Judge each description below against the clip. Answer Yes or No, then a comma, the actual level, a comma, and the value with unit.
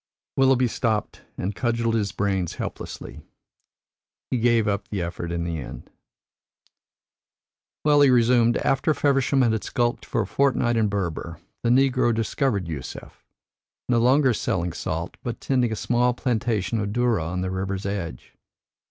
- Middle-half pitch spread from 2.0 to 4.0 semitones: No, average, 4.6 semitones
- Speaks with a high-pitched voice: No, low, 115 Hz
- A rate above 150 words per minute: No, average, 145 wpm